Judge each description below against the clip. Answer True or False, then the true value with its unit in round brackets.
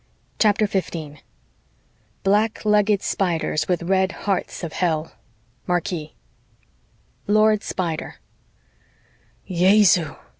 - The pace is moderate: False (80 wpm)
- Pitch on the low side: False (185 Hz)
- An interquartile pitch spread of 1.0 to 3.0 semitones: False (3.6 semitones)